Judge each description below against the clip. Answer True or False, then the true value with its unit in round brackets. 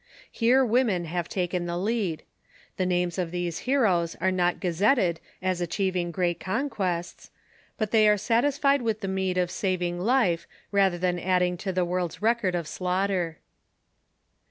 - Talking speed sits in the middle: True (155 wpm)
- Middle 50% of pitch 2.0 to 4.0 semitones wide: True (3.3 semitones)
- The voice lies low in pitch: False (185 Hz)